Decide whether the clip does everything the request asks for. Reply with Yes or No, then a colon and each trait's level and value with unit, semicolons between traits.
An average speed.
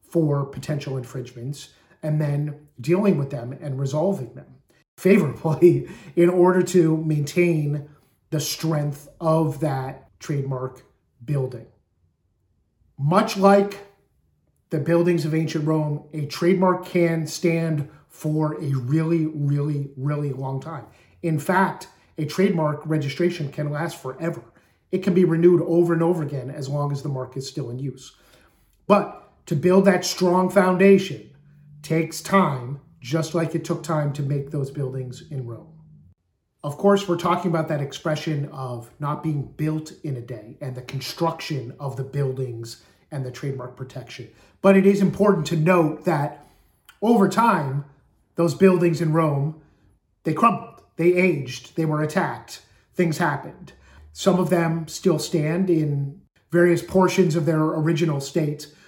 Yes: average, 145 wpm